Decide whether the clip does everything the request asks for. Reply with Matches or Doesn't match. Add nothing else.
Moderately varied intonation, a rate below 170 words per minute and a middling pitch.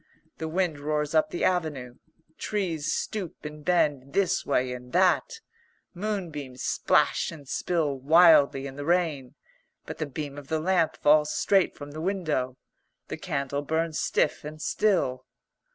Matches